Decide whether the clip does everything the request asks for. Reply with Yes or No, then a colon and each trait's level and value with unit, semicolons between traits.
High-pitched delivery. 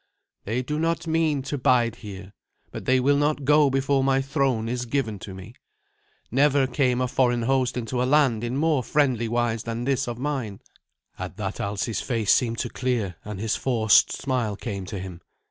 No: low, 125 Hz